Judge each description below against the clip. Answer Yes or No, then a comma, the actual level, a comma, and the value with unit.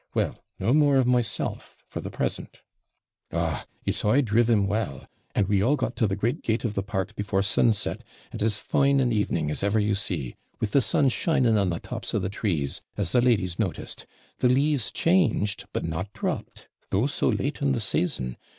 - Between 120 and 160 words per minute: No, average, 200 wpm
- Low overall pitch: Yes, low, 105 Hz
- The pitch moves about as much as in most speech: Yes, average, 4.5 semitones